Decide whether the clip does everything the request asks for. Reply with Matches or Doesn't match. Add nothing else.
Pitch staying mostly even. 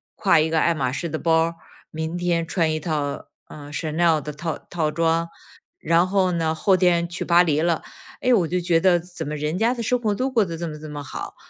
Matches